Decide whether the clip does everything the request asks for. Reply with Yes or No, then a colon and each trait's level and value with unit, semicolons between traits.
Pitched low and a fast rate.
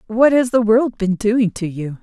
No: high, 220 Hz; fast, 235 wpm